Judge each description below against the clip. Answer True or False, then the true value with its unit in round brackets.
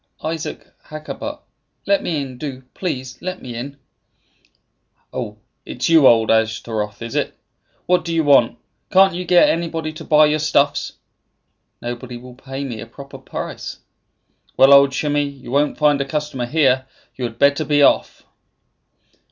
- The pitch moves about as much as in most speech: True (3.5 semitones)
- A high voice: False (140 Hz)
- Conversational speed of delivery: True (160 wpm)